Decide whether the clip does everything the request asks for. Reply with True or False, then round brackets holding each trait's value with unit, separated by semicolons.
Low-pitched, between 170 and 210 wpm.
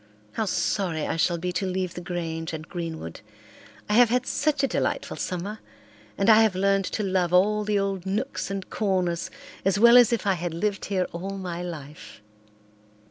False (190 Hz; 190 wpm)